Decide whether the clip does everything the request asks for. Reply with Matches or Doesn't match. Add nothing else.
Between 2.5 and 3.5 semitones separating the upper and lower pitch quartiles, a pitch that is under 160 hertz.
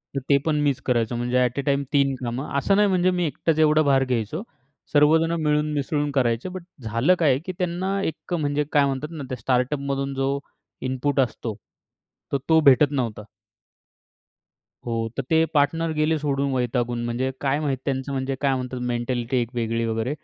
Matches